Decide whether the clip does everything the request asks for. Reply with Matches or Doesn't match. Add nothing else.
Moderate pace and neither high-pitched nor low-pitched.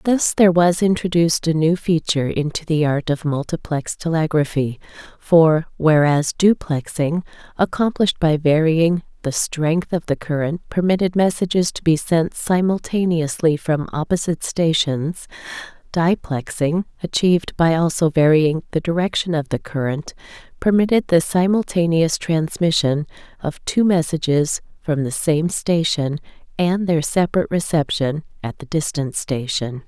Doesn't match